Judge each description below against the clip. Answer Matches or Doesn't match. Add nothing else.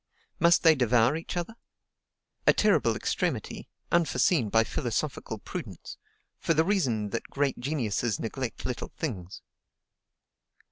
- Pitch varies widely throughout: Matches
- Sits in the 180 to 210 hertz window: Doesn't match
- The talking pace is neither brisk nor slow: Doesn't match